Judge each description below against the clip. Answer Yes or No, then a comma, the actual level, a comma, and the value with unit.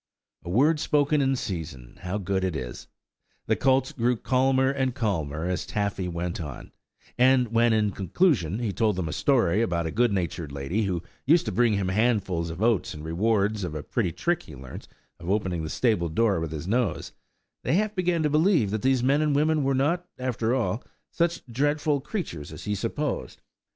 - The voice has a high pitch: No, low, 110 Hz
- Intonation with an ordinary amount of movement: No, wide, 7.2 semitones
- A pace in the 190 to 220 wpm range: Yes, average, 195 wpm